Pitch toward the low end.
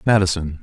Yes: very low, 90 Hz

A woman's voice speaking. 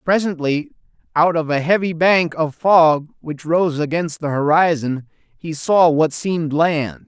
No: male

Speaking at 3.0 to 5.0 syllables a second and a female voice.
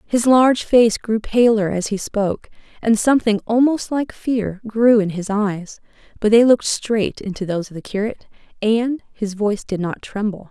Yes: 4.9 syllables/s; female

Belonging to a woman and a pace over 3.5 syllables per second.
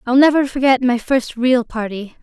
Yes: female; 4.8 syllables/s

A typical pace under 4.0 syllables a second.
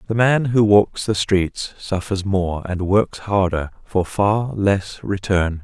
Yes: 3.5 syllables/s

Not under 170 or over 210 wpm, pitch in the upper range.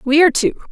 No: fast, 250 wpm; very high, 315 Hz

